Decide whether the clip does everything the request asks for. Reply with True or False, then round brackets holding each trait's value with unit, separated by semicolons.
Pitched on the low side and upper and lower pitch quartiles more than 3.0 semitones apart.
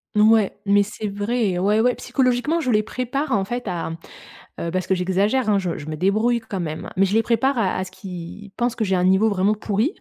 False (205 Hz; 3.9 semitones)